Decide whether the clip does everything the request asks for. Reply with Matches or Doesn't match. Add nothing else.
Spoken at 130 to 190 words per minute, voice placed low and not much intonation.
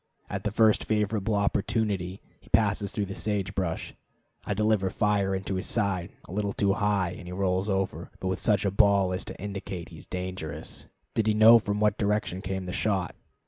Doesn't match